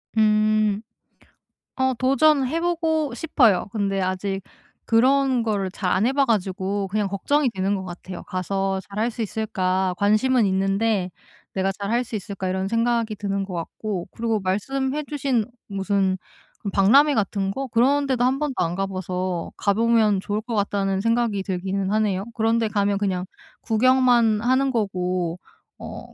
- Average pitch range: Yes, average, 3.9 semitones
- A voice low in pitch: No, high, 210 Hz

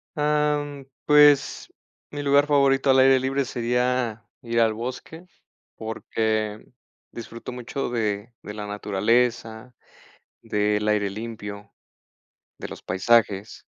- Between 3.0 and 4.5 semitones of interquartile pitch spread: Yes, average, 4.1 semitones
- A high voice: No, low, 115 Hz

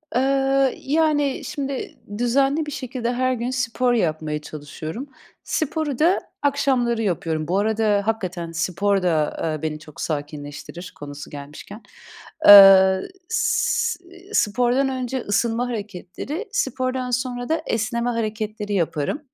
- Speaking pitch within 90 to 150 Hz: No, high, 235 Hz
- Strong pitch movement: Yes, wide, 6.9 semitones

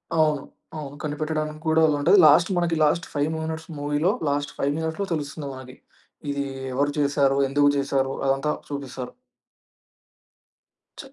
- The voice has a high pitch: No, medium, 145 Hz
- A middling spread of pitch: No, narrow, 2.1 semitones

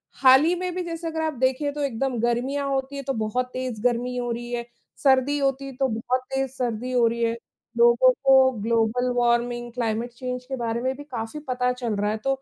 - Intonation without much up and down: Yes, narrow, 2.3 semitones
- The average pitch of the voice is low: No, very high, 250 Hz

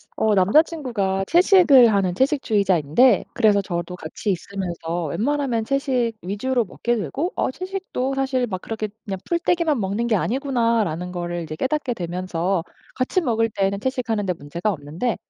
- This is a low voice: No, high, 215 Hz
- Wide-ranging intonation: Yes, wide, 6.3 semitones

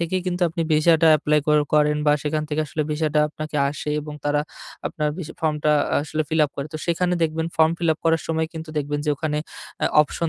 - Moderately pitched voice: Yes, medium, 155 Hz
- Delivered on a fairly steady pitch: Yes, narrow, 1.5 semitones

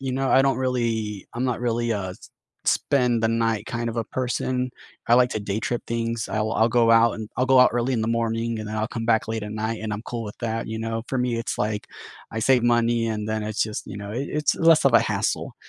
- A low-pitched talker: Yes, low, 115 Hz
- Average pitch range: No, narrow, 1.8 semitones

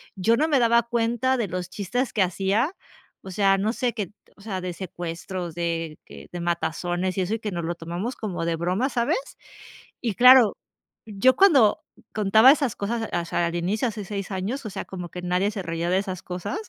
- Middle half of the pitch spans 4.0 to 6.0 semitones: Yes, average, 4.7 semitones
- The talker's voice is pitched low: No, high, 195 Hz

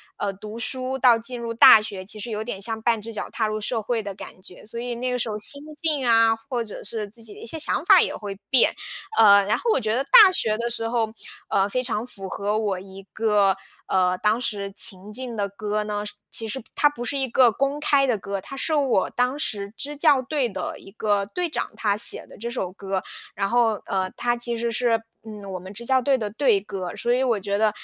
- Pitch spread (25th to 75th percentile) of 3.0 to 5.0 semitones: Yes, average, 3.5 semitones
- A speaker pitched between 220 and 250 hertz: Yes, high, 225 Hz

